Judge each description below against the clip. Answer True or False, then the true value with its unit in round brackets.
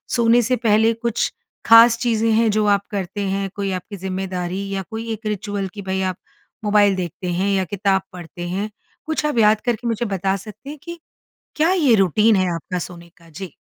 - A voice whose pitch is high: True (205 Hz)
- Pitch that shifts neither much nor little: True (3.2 semitones)